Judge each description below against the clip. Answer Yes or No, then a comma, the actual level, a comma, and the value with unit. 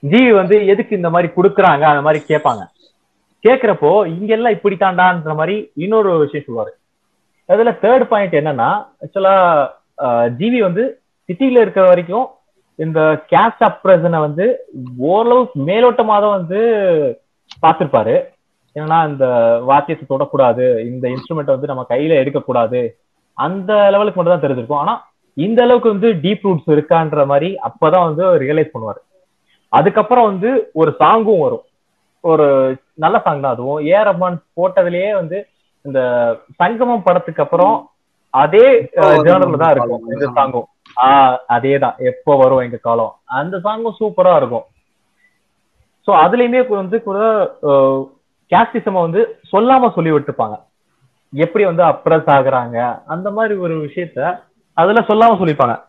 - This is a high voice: No, medium, 180 Hz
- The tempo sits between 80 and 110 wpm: No, average, 125 wpm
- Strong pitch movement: Yes, wide, 6.7 semitones